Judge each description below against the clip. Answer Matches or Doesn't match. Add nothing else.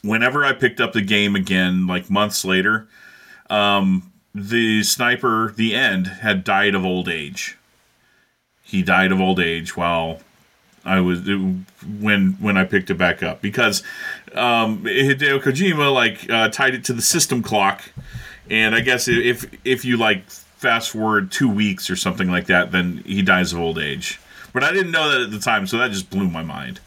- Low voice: Matches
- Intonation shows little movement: Doesn't match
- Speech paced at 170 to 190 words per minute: Matches